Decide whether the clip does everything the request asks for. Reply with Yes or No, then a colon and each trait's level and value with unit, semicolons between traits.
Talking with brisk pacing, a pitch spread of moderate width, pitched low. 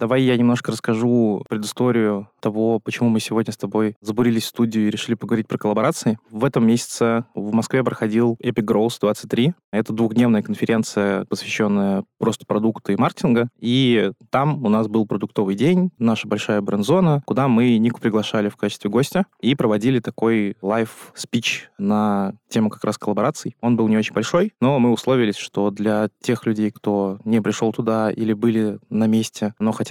No: fast, 170 wpm; narrow, 2.0 semitones; low, 110 Hz